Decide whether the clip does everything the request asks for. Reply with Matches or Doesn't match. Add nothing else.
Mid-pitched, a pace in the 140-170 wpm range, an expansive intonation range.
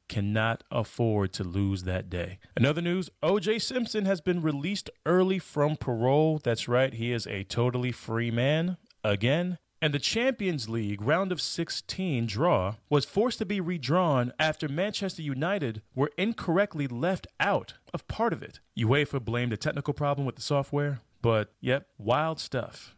Matches